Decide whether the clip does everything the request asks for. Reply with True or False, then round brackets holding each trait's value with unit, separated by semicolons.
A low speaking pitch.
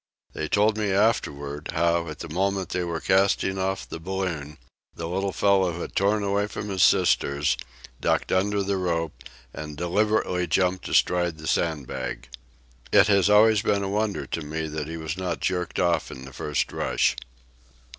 True (90 Hz)